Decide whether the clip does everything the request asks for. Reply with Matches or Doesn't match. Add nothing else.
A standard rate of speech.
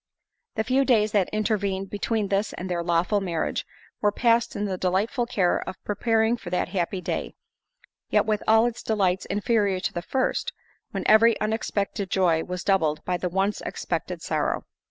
Matches